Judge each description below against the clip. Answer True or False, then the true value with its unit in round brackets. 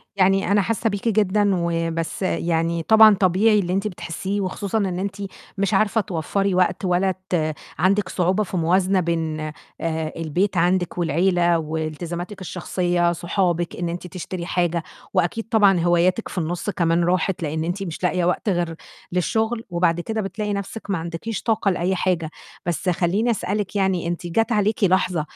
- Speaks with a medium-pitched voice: True (180 Hz)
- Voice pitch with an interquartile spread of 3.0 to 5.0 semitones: False (2.6 semitones)